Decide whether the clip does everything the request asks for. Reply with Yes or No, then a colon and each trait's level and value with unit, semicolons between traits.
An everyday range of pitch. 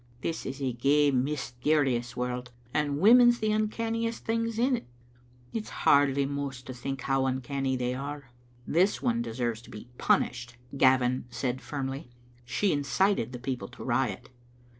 Yes: average, 3.8 semitones